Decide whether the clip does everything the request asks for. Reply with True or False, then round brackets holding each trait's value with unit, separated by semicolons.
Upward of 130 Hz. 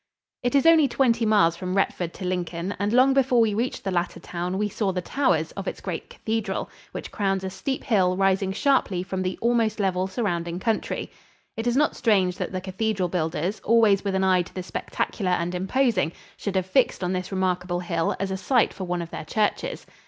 True (190 Hz)